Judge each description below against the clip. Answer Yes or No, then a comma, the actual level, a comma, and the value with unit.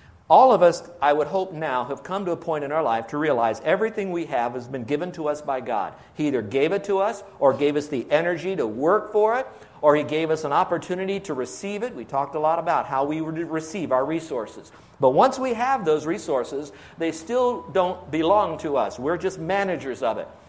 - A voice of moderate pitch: Yes, medium, 160 Hz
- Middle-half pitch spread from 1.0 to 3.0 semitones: No, average, 4.5 semitones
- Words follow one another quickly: Yes, fast, 230 wpm